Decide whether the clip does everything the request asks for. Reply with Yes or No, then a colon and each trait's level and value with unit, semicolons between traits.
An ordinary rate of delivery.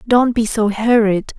Yes: average, 175 wpm